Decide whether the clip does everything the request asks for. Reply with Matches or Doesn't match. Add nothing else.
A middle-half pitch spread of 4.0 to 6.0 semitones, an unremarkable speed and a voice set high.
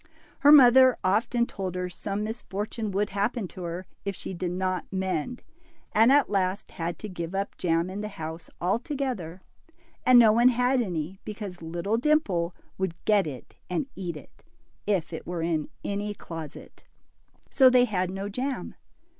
Matches